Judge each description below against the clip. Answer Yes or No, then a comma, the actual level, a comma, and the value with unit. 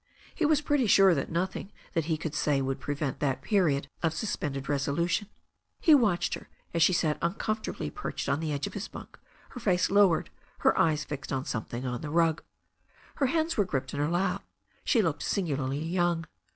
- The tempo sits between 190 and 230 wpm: Yes, average, 195 wpm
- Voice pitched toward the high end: No, medium, 165 Hz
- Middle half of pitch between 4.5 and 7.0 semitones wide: Yes, wide, 5.4 semitones